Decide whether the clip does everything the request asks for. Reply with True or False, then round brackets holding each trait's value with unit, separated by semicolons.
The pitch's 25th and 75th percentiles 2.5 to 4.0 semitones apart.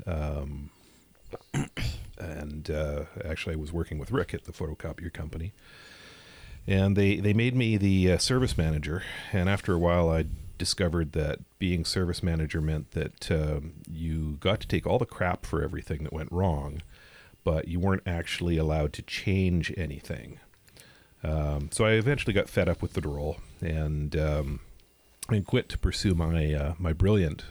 True (3.6 semitones)